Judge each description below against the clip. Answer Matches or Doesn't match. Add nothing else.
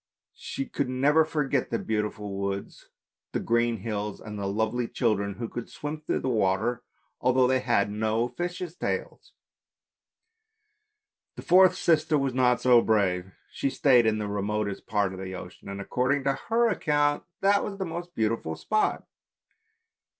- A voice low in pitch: Matches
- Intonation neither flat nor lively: Doesn't match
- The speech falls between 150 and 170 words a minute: Matches